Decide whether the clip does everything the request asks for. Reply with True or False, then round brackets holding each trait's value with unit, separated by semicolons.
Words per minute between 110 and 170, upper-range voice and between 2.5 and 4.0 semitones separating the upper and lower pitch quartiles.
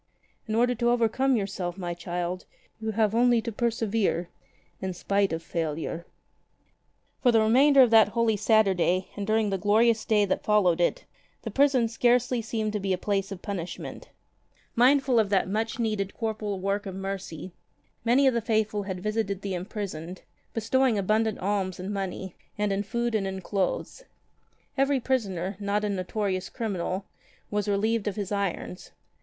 True (160 wpm; 205 Hz; 3.0 semitones)